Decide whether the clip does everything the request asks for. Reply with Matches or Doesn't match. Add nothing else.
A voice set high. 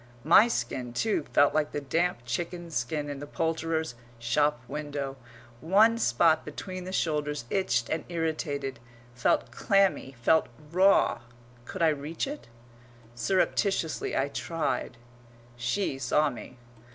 Doesn't match